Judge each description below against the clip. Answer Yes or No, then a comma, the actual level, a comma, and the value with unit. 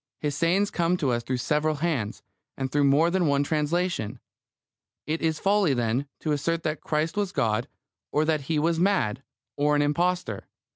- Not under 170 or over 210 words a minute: Yes, average, 180 wpm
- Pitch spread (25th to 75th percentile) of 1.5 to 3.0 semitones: No, average, 3.4 semitones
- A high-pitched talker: No, medium, 150 Hz